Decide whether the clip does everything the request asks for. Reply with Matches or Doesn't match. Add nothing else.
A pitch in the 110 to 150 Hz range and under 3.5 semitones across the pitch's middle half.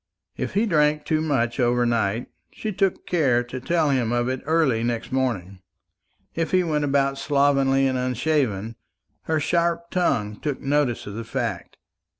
Doesn't match